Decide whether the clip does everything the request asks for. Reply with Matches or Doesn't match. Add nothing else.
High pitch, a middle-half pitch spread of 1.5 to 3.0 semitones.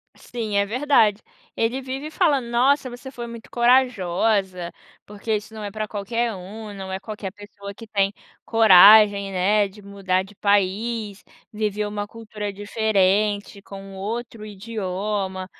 Matches